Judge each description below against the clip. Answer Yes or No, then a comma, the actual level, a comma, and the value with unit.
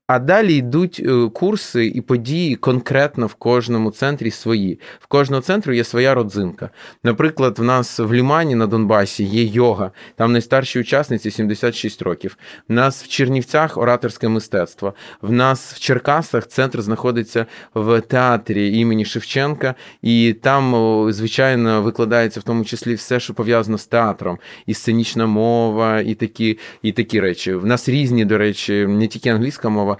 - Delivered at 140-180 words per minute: Yes, average, 150 wpm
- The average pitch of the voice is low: Yes, low, 115 Hz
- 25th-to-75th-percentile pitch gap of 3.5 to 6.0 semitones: No, average, 2.7 semitones